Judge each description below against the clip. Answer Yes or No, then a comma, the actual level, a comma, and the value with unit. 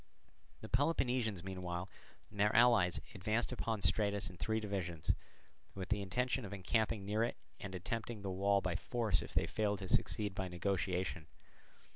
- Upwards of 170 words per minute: No, average, 160 wpm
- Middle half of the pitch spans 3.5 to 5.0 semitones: No, average, 3.1 semitones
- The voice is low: Yes, low, 100 Hz